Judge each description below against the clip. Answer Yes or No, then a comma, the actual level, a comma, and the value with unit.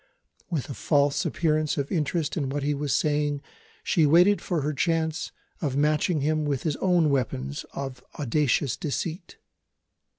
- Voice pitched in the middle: Yes, medium, 150 Hz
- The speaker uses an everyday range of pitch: No, narrow, 2.3 semitones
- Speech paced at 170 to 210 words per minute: No, average, 155 wpm